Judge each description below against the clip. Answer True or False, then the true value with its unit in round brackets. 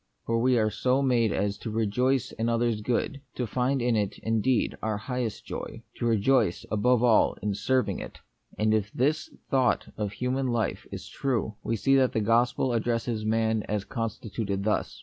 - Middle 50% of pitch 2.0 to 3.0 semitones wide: True (2.6 semitones)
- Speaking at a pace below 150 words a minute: False (180 wpm)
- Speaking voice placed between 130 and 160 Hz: False (115 Hz)